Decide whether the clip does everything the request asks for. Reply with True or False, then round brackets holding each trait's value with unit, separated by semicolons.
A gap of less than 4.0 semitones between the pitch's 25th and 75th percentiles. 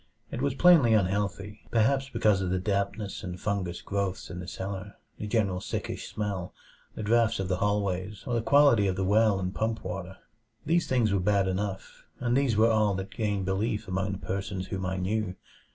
True (2.7 semitones)